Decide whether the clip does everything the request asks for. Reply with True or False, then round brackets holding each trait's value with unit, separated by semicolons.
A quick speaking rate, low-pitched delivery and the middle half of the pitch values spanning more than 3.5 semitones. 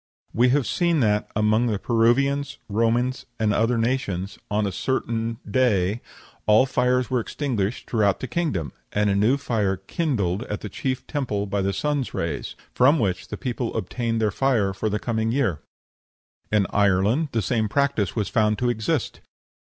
False (170 wpm; 115 Hz; 3.9 semitones)